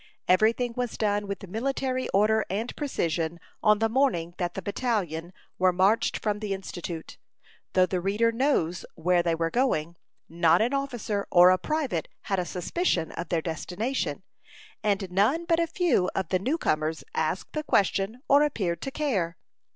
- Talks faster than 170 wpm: No, average, 165 wpm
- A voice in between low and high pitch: No, high, 200 Hz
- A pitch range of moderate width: No, wide, 6.1 semitones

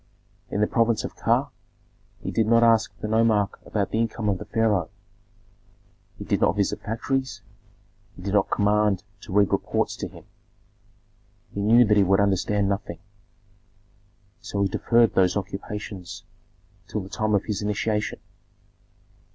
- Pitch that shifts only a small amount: Yes, narrow, 2.0 semitones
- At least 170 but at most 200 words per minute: No, average, 150 wpm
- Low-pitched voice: Yes, low, 105 Hz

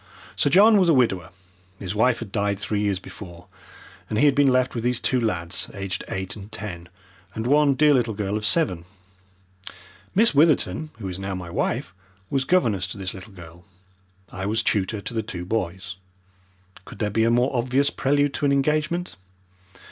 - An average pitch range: No, wide, 6.1 semitones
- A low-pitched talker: Yes, low, 110 Hz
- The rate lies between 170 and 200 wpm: Yes, average, 185 wpm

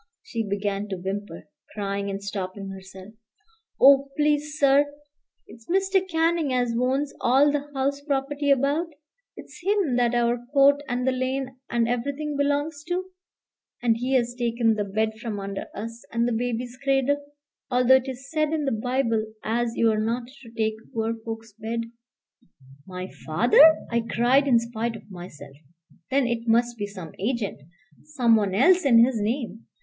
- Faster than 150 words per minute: Yes, average, 160 wpm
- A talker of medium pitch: No, high, 240 Hz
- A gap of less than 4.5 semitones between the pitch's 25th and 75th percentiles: Yes, average, 4.1 semitones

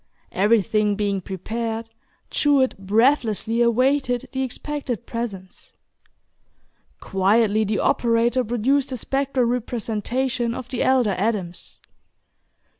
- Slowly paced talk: Yes, slow, 95 wpm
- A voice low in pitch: No, high, 230 Hz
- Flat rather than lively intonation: No, average, 3.4 semitones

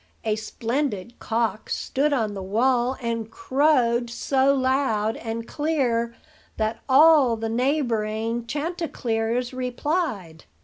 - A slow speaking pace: Yes, slow, 105 wpm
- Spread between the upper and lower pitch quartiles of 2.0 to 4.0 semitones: Yes, average, 3.5 semitones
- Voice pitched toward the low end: No, high, 240 Hz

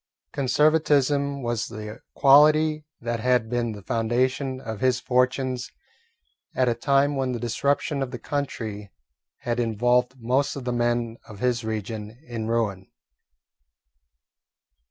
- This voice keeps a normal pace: No, slow, 130 wpm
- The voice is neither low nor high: No, low, 125 Hz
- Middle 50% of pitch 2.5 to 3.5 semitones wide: Yes, average, 3.0 semitones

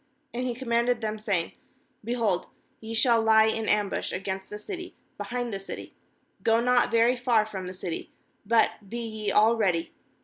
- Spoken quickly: No, average, 170 wpm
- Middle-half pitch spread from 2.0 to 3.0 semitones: Yes, narrow, 2.4 semitones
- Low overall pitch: No, high, 225 Hz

